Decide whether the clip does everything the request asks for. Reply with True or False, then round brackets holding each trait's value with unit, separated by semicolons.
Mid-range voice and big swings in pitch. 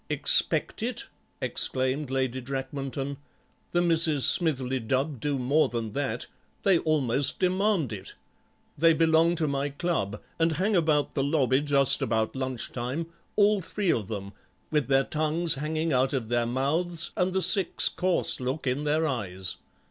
False (145 Hz; 4.0 semitones)